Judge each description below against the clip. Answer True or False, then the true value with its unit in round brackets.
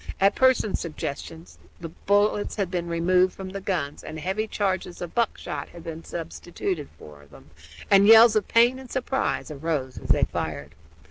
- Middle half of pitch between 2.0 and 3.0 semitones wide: False (4.1 semitones)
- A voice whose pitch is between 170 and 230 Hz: True (185 Hz)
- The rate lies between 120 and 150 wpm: False (165 wpm)